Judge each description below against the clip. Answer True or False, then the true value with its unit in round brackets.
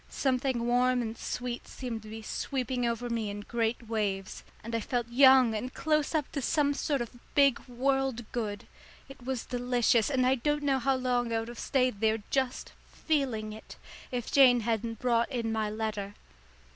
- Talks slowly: False (185 wpm)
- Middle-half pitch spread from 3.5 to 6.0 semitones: False (2.8 semitones)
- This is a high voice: True (245 Hz)